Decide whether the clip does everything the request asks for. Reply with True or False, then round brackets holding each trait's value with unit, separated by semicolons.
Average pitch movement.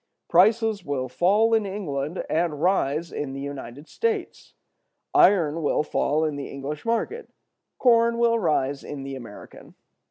False (7.8 semitones)